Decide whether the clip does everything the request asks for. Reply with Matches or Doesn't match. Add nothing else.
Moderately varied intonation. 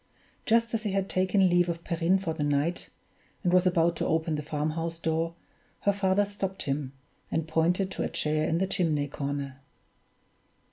Matches